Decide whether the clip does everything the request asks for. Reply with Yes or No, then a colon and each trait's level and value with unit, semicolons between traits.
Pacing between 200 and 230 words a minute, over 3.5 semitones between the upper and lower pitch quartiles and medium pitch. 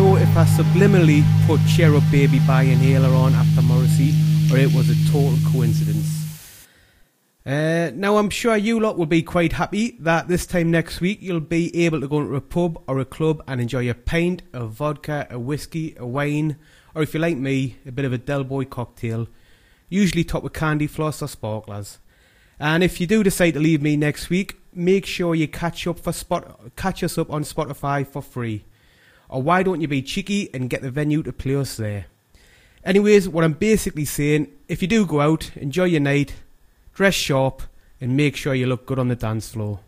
Yes: fast, 205 wpm; average, 3.9 semitones; medium, 150 Hz